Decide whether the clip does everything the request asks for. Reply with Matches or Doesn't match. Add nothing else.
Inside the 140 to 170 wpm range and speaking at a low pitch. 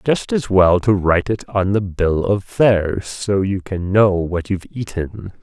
Doesn't match